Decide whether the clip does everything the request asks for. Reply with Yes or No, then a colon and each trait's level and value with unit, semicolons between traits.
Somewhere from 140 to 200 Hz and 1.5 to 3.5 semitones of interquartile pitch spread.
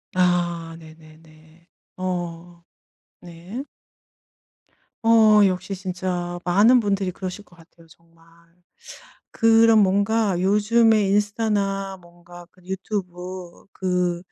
Yes: medium, 185 Hz; average, 2.9 semitones